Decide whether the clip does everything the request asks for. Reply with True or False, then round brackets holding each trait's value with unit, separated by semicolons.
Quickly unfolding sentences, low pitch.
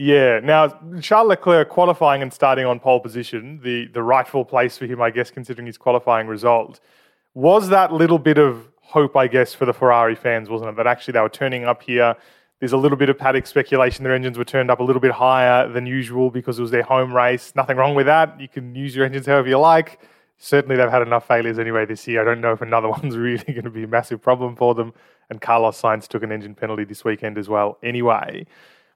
True (235 wpm; 125 Hz)